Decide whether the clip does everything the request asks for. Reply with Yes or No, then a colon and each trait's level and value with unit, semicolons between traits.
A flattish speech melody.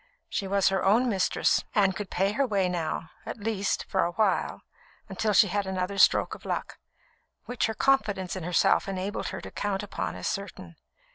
Yes: narrow, 1.8 semitones